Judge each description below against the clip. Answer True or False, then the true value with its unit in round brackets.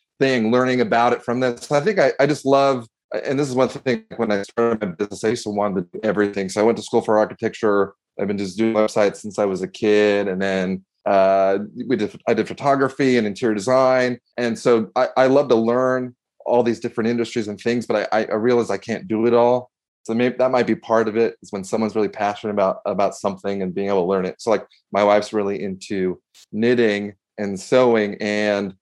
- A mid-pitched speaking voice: False (110 Hz)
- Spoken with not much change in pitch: False (3.3 semitones)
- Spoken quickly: True (230 wpm)